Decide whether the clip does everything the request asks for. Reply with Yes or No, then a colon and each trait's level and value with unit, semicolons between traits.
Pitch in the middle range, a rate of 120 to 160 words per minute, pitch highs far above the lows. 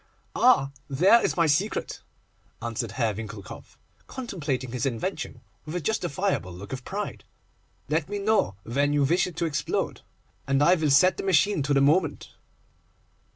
Yes: medium, 145 Hz; average, 155 wpm; wide, 5.9 semitones